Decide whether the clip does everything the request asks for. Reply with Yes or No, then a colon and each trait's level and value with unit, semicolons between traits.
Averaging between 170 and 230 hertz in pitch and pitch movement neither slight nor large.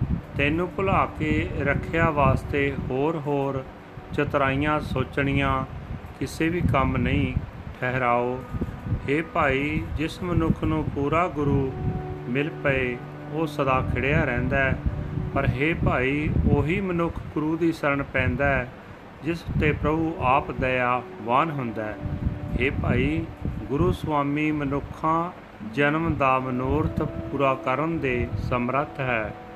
No: medium, 140 Hz; average, 3.2 semitones